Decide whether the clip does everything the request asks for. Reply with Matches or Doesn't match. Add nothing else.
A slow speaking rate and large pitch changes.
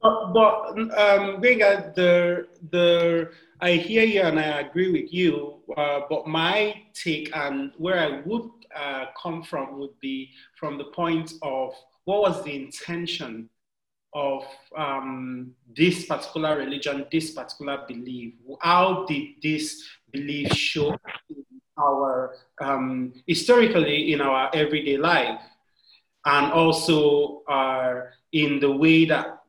Doesn't match